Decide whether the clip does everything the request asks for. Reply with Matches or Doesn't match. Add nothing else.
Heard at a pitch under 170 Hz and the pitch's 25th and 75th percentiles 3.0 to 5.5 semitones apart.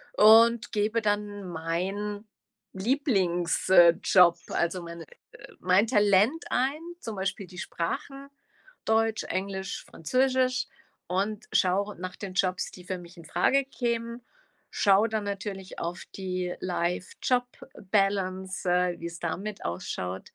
Doesn't match